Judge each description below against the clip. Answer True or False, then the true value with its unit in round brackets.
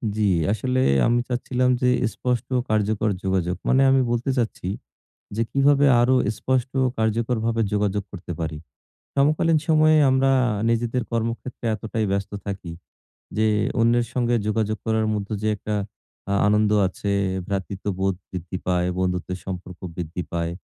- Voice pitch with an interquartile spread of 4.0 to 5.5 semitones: True (4.3 semitones)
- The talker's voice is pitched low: True (110 Hz)